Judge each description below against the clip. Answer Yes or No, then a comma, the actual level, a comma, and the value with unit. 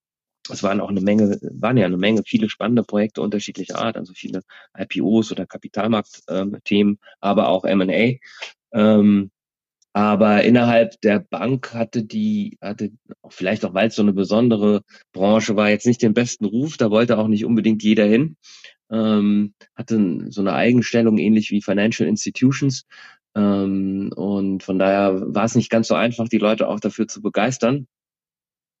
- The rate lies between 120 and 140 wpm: No, average, 160 wpm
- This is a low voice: Yes, low, 110 Hz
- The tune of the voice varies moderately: No, narrow, 2.0 semitones